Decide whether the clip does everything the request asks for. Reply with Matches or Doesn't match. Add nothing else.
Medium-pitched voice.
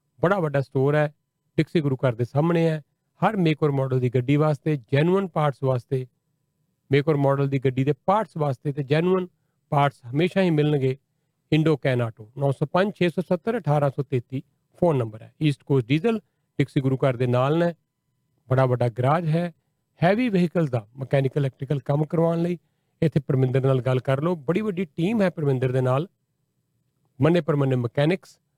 Matches